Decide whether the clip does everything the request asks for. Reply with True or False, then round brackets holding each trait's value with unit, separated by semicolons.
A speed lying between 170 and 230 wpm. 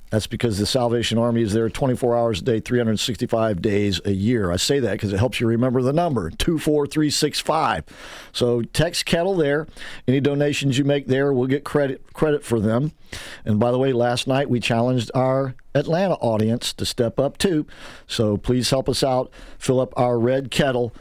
True (190 wpm)